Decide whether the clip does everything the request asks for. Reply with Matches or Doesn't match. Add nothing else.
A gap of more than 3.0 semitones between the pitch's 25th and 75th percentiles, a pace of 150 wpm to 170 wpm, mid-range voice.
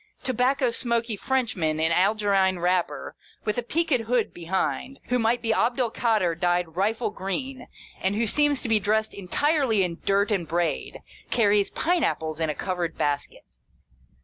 Doesn't match